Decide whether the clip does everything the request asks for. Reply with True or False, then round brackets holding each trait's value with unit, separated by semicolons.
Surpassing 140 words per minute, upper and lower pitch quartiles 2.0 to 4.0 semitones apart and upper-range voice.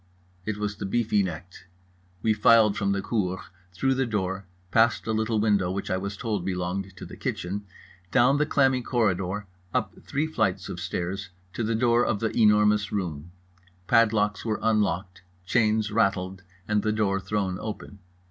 False (170 wpm; 2.7 semitones; 105 Hz)